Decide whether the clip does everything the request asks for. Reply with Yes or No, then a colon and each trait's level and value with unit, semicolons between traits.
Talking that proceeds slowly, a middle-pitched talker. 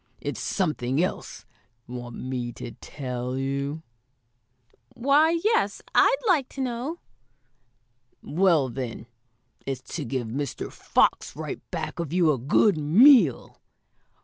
Yes: slow, 120 wpm; medium, 150 Hz